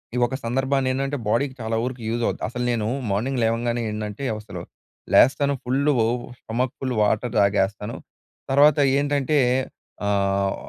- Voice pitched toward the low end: Yes, low, 120 Hz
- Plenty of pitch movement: No, average, 4.1 semitones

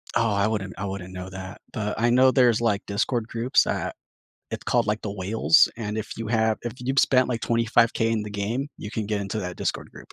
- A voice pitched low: Yes, low, 110 Hz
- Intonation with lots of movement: No, average, 2.7 semitones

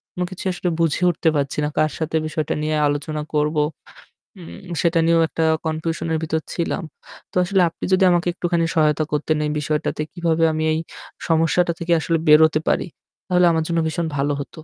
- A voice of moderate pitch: Yes, medium, 160 Hz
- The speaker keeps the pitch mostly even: Yes, narrow, 1.9 semitones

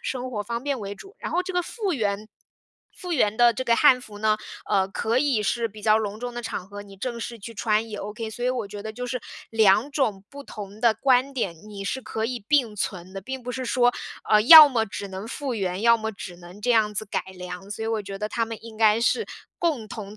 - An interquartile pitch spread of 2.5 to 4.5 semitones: Yes, average, 3.3 semitones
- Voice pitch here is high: Yes, high, 220 Hz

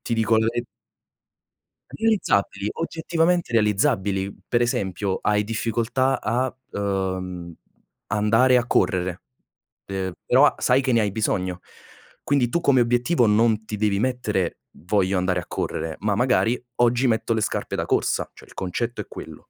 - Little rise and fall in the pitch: No, average, 4.1 semitones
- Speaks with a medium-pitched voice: No, low, 110 Hz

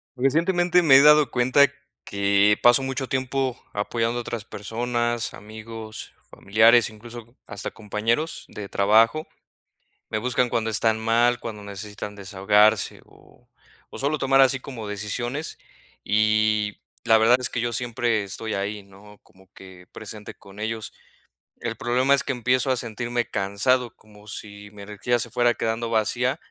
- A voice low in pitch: Yes, low, 115 Hz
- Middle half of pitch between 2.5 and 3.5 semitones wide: Yes, average, 2.9 semitones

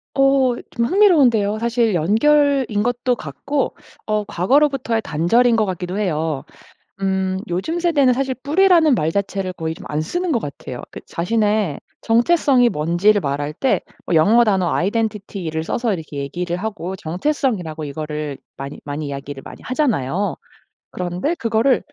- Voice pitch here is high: Yes, high, 210 Hz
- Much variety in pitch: Yes, wide, 7.3 semitones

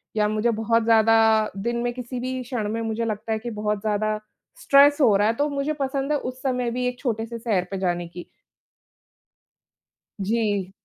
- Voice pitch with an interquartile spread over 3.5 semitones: No, average, 2.8 semitones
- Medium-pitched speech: No, high, 225 Hz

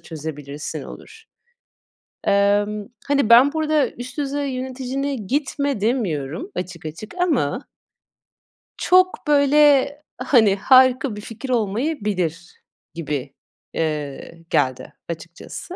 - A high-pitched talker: Yes, high, 235 Hz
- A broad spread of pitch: Yes, wide, 8.7 semitones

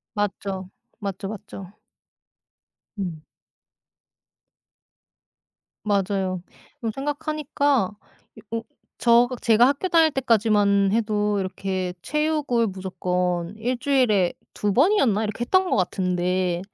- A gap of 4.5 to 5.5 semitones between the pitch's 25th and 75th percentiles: Yes, average, 5.2 semitones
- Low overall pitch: No, high, 210 Hz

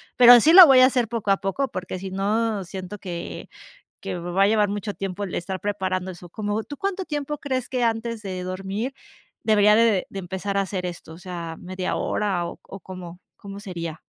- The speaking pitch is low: No, high, 195 Hz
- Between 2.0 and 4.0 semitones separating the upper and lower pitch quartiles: Yes, average, 3.6 semitones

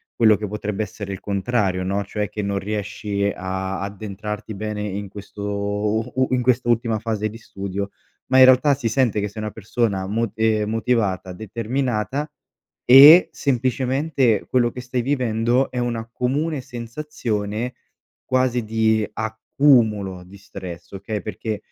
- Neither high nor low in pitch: No, low, 110 Hz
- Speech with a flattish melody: No, average, 3.4 semitones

